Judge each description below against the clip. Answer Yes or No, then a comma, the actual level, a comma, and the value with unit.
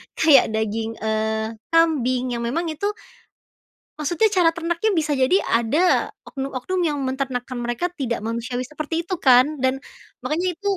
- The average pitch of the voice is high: Yes, very high, 265 Hz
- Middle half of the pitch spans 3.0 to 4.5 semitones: No, average, 5.2 semitones